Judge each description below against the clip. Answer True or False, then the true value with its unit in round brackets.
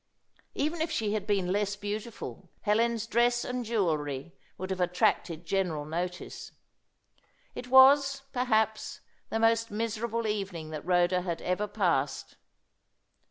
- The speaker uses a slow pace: True (125 wpm)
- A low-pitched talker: False (205 Hz)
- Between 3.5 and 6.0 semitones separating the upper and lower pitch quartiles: True (4.5 semitones)